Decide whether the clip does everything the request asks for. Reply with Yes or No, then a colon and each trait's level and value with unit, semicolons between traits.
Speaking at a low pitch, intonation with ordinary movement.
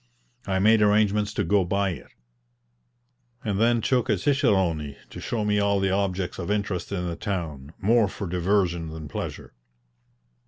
Yes: low, 100 Hz; average, 3.0 semitones